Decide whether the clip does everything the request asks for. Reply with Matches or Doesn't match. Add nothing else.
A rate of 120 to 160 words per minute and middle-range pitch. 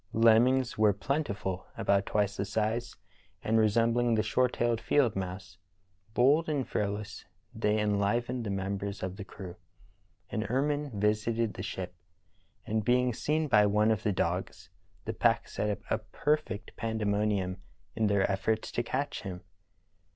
Doesn't match